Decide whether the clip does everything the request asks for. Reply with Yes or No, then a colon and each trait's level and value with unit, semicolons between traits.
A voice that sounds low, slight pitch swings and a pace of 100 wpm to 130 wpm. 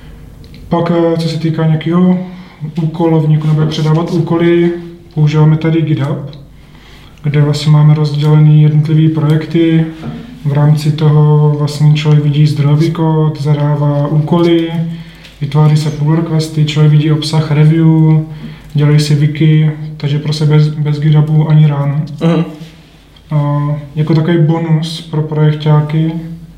No: medium, 155 Hz; narrow, 1.3 semitones; slow, 115 wpm